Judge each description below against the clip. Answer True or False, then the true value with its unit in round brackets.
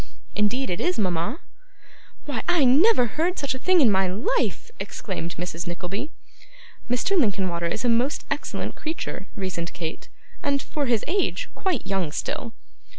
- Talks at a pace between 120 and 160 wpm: True (150 wpm)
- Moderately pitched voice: False (230 Hz)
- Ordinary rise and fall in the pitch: False (8.5 semitones)